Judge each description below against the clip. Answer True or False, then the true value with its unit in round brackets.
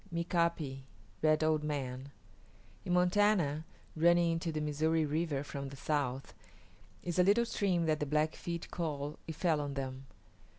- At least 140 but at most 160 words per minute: True (145 wpm)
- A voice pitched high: False (155 Hz)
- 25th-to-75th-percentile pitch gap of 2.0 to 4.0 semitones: True (2.9 semitones)